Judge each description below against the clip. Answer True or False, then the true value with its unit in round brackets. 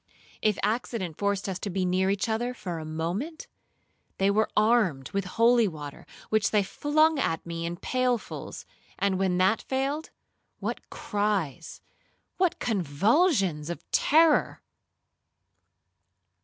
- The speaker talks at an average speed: False (125 wpm)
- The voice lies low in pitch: False (200 Hz)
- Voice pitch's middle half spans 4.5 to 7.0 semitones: True (5.3 semitones)